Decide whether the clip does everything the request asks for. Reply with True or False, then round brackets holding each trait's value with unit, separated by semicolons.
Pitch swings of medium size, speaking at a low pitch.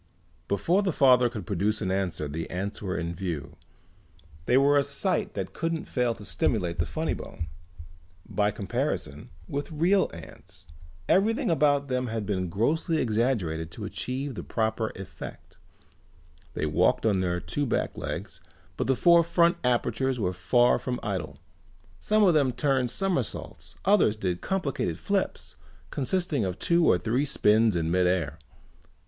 False (7.6 semitones; 115 Hz)